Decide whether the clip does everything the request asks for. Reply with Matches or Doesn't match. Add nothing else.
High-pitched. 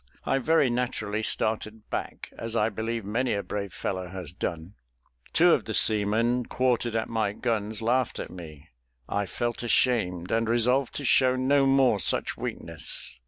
Doesn't match